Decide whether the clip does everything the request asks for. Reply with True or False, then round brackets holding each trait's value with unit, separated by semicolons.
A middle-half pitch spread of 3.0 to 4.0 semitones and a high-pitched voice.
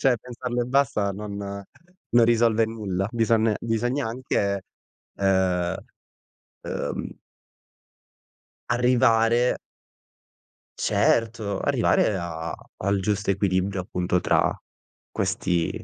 False (3.6 semitones; 110 Hz)